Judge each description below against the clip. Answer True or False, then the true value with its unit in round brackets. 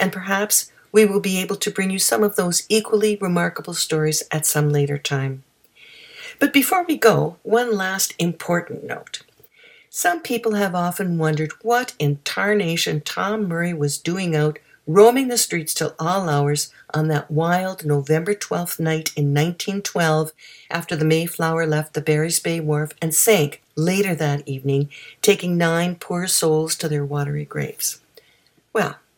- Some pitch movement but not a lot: True (4.6 semitones)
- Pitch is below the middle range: False (170 Hz)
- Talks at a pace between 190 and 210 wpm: False (155 wpm)